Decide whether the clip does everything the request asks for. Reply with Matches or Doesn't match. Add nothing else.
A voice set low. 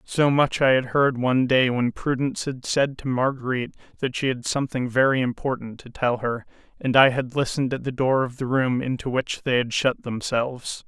Matches